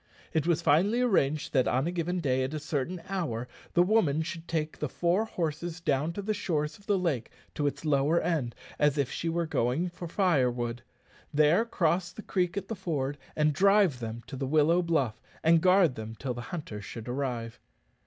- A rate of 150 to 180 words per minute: No, average, 195 wpm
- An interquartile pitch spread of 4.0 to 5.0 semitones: Yes, average, 4.7 semitones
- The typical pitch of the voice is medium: Yes, medium, 155 Hz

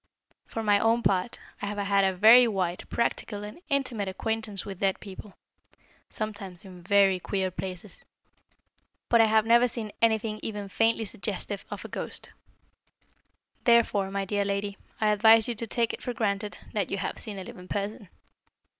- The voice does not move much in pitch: Yes, narrow, 2.3 semitones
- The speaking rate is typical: Yes, average, 170 wpm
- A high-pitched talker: Yes, high, 205 Hz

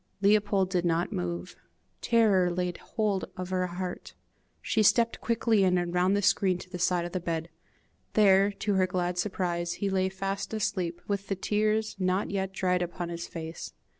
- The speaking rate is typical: Yes, average, 180 wpm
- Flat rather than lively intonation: Yes, narrow, 2.2 semitones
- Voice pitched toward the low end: No, medium, 185 Hz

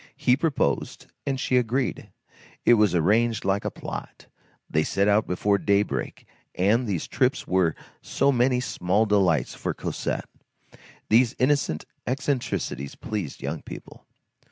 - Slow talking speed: Yes, slow, 130 wpm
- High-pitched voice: No, low, 105 Hz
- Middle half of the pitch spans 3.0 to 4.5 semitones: No, average, 5.2 semitones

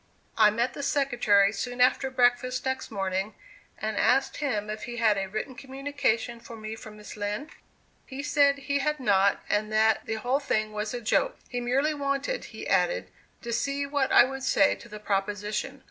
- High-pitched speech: Yes, high, 240 Hz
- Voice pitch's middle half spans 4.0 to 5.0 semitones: Yes, average, 4.4 semitones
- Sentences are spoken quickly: No, average, 190 wpm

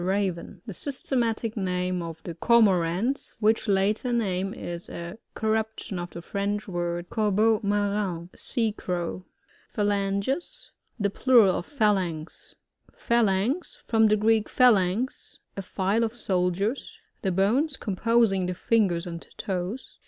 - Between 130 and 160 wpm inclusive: Yes, average, 140 wpm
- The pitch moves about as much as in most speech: Yes, average, 3.7 semitones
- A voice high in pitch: Yes, high, 200 Hz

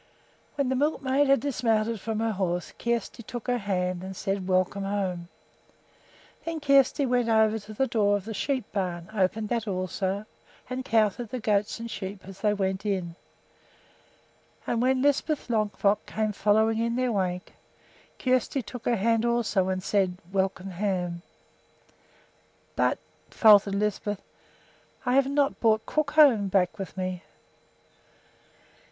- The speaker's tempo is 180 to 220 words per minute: No, average, 145 wpm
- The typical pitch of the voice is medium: No, high, 215 Hz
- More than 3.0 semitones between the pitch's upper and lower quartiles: Yes, average, 4.0 semitones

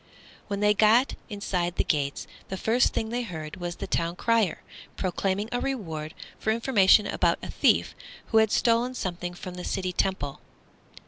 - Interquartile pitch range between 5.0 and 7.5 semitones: No, average, 4.1 semitones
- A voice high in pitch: Yes, high, 195 Hz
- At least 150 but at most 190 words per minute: Yes, average, 170 wpm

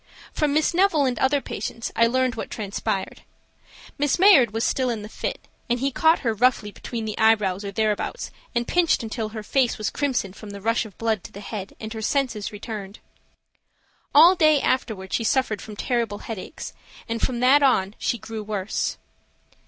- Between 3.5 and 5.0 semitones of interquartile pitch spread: Yes, average, 3.8 semitones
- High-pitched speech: Yes, high, 230 Hz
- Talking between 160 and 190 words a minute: Yes, average, 185 wpm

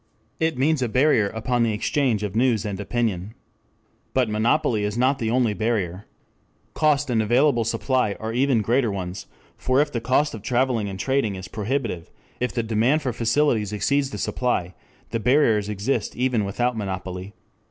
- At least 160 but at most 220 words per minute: Yes, average, 170 wpm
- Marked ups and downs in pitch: No, average, 3.8 semitones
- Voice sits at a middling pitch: No, low, 115 Hz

